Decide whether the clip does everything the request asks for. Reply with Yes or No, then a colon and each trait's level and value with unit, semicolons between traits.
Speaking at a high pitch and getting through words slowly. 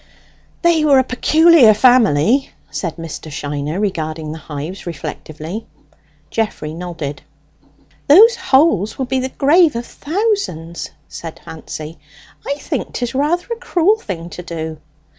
Yes: high, 210 Hz; slow, 130 wpm